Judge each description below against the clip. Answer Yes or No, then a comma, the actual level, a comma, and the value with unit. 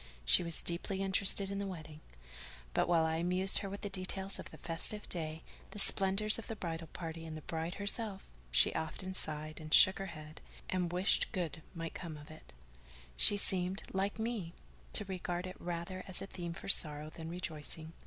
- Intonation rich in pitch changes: No, average, 3.2 semitones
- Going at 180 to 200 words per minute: Yes, average, 195 wpm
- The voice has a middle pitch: Yes, medium, 175 Hz